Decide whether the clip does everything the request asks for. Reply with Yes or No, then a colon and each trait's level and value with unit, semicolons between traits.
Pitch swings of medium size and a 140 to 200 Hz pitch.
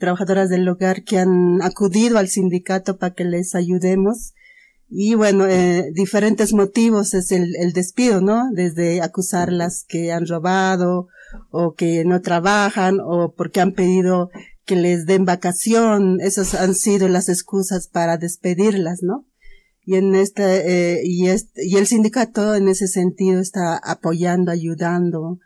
No: narrow, 2.0 semitones; medium, 185 Hz